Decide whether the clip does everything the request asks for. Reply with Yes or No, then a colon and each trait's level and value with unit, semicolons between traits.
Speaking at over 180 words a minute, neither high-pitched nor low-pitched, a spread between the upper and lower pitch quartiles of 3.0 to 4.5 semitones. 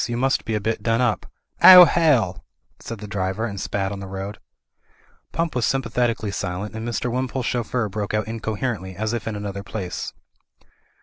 No: average, 195 wpm; low, 110 Hz; average, 3.3 semitones